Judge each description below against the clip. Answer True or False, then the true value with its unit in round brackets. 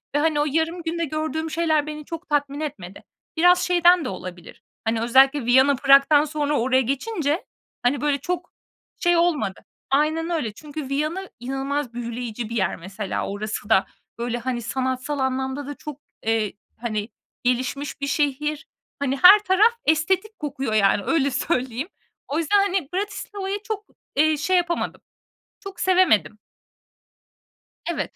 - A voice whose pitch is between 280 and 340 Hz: True (290 Hz)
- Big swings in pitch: False (4.9 semitones)